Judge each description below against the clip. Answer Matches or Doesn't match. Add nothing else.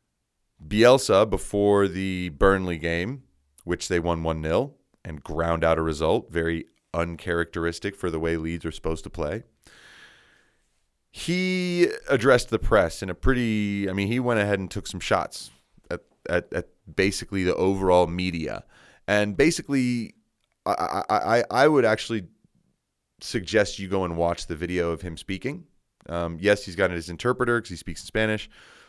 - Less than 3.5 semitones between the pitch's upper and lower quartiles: Doesn't match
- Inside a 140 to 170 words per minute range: Matches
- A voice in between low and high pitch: Doesn't match